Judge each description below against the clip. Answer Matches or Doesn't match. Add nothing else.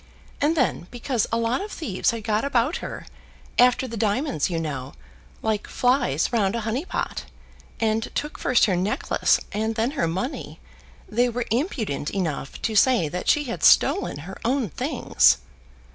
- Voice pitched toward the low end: Doesn't match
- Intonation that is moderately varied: Matches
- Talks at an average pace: Matches